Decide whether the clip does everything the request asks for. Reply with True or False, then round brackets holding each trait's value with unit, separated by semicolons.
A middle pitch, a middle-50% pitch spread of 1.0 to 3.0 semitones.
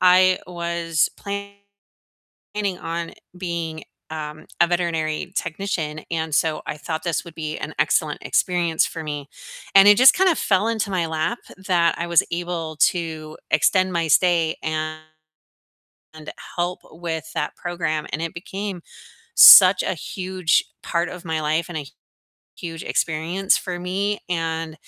True (170 Hz; 2.4 semitones)